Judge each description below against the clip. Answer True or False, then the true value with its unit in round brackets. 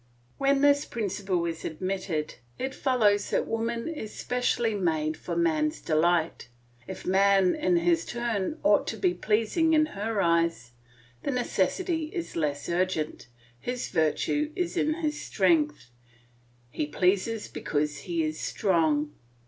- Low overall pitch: False (190 Hz)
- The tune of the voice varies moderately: False (7.1 semitones)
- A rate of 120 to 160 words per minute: True (135 wpm)